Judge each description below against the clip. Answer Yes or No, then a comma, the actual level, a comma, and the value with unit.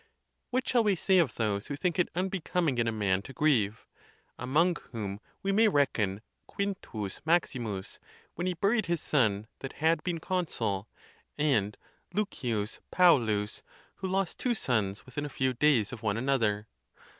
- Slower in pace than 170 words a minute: Yes, average, 160 wpm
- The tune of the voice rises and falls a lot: Yes, wide, 8.7 semitones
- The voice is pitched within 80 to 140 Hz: Yes, low, 135 Hz